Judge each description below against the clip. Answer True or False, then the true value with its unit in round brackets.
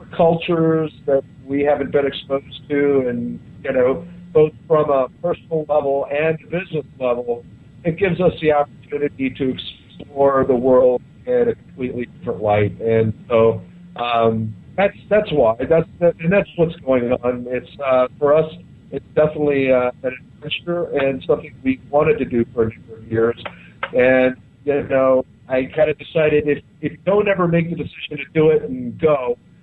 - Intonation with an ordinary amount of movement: True (4.0 semitones)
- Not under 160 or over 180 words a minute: True (170 wpm)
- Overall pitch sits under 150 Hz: True (140 Hz)